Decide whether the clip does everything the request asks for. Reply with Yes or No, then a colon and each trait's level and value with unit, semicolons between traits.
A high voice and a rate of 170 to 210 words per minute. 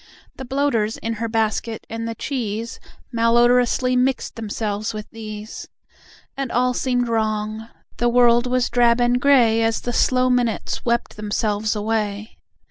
No: high, 230 Hz; average, 140 wpm